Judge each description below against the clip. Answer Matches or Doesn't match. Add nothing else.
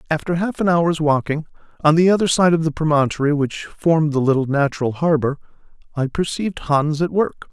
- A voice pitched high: Doesn't match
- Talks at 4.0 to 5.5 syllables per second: Doesn't match